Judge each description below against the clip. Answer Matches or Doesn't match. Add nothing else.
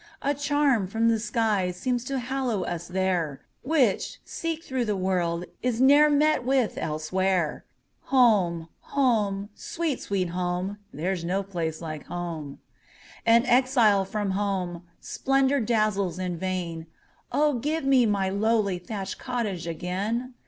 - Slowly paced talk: Matches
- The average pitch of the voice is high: Matches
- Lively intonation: Matches